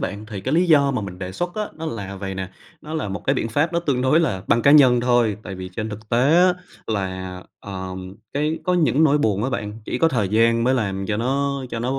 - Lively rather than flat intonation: Yes, wide, 6.2 semitones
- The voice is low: Yes, low, 120 Hz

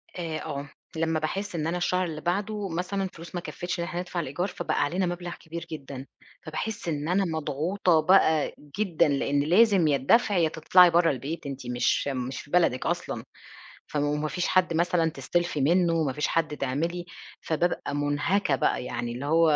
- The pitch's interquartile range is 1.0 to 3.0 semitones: No, average, 3.4 semitones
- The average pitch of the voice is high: No, medium, 165 Hz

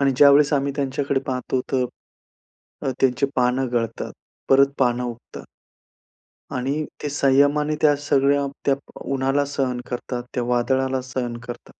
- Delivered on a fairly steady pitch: Yes, narrow, 2.0 semitones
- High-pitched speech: No, low, 135 Hz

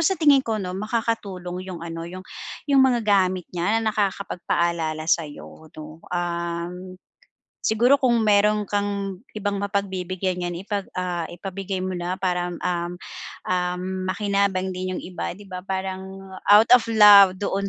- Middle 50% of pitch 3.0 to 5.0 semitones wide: No, narrow, 2.4 semitones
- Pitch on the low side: No, high, 190 Hz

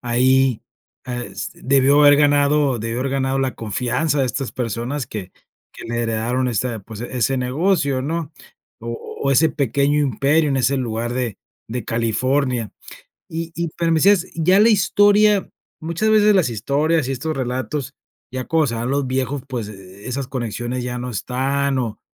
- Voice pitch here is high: No, low, 130 Hz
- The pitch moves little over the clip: No, average, 3.5 semitones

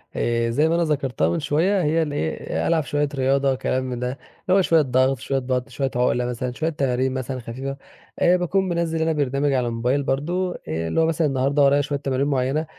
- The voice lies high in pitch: No, low, 135 Hz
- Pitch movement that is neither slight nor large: Yes, average, 3.6 semitones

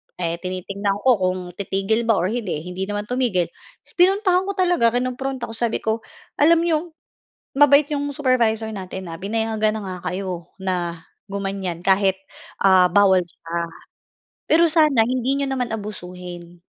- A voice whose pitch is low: No, high, 210 Hz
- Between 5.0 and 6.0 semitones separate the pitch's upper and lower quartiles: Yes, wide, 5.6 semitones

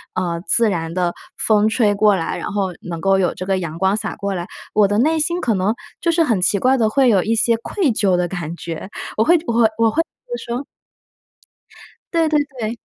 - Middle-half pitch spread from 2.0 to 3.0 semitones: No, average, 4.3 semitones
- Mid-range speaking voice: No, high, 210 Hz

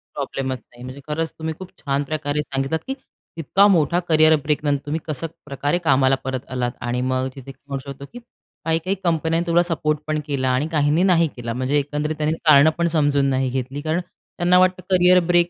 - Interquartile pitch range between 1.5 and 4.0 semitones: Yes, average, 3.4 semitones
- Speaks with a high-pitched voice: No, medium, 150 Hz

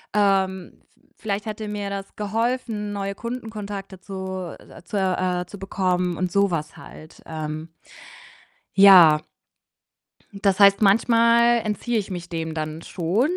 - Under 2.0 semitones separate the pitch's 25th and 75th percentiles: No, average, 2.8 semitones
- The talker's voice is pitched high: Yes, high, 195 Hz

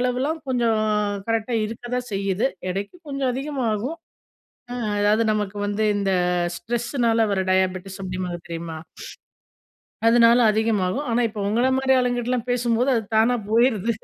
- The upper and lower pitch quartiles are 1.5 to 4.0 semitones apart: Yes, average, 3.4 semitones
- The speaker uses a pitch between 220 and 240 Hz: Yes, high, 230 Hz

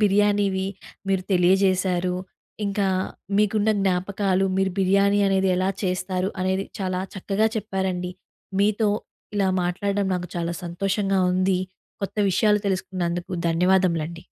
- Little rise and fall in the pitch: Yes, narrow, 1.5 semitones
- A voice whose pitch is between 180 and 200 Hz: Yes, high, 190 Hz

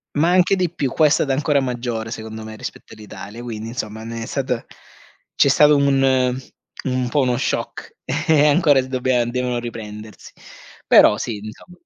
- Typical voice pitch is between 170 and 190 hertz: No, low, 125 Hz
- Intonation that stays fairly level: No, average, 3.9 semitones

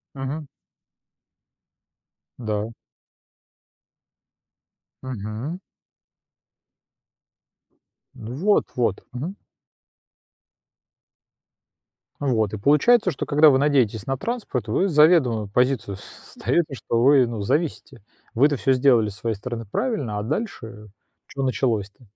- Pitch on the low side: Yes, low, 125 Hz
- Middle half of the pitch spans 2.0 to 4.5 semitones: No, average, 4.9 semitones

